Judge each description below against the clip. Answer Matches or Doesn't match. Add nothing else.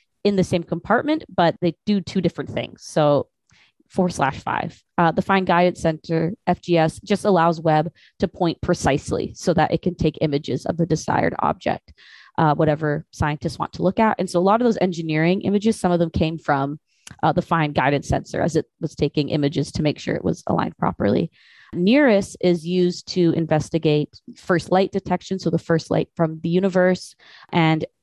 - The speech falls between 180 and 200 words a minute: Matches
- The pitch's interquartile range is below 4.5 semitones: Matches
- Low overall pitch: Doesn't match